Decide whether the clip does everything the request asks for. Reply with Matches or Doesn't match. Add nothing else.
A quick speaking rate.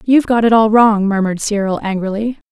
Doesn't match